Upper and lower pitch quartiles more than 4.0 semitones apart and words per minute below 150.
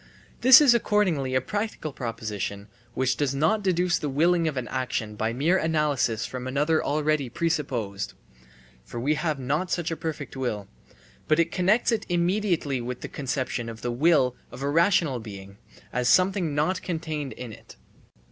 No: wide, 5.4 semitones; average, 165 wpm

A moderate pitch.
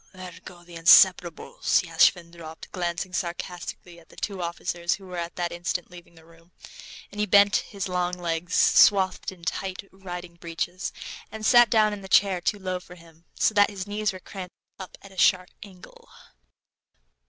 Yes: medium, 180 Hz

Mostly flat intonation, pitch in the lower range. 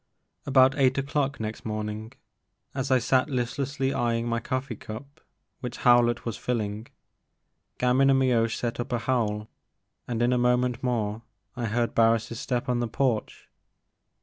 Yes: narrow, 2.2 semitones; low, 120 Hz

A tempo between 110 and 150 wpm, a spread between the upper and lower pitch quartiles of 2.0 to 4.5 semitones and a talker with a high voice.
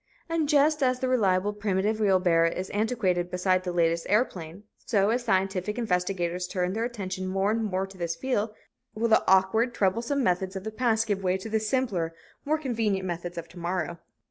No: average, 190 wpm; average, 3.7 semitones; high, 195 Hz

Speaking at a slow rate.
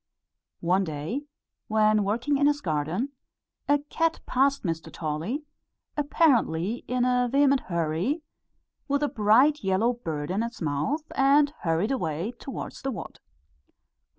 Yes: slow, 130 wpm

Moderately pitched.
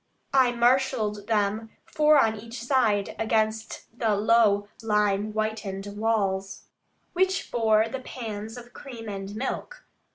No: high, 220 Hz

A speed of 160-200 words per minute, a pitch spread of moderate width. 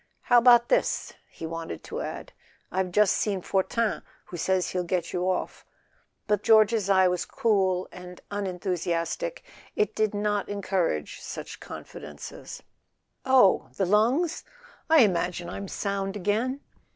No: slow, 135 wpm; average, 3.2 semitones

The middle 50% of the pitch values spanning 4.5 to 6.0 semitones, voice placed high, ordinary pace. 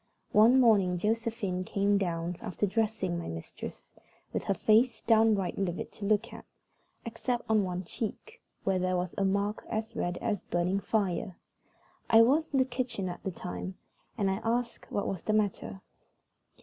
No: average, 3.6 semitones; high, 205 Hz; average, 165 wpm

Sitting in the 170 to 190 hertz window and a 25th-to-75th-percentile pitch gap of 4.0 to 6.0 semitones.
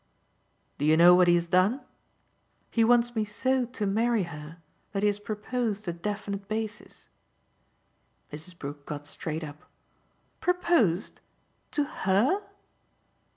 No: high, 205 Hz; wide, 5.5 semitones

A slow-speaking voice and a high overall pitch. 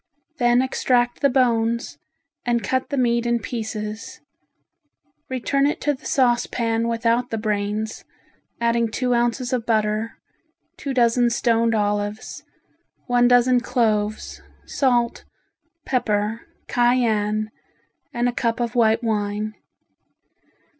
Yes: slow, 115 wpm; high, 235 Hz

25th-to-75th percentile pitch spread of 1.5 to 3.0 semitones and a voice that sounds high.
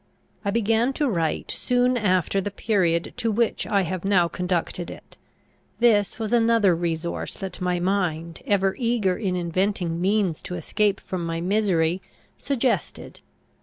No: average, 4.0 semitones; high, 195 Hz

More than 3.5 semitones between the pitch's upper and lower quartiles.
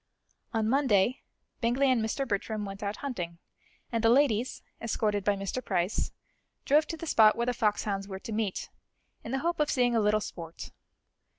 Yes: average, 3.9 semitones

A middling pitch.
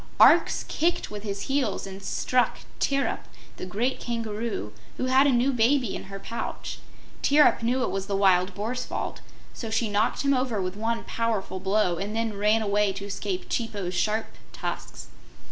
No: high, 215 Hz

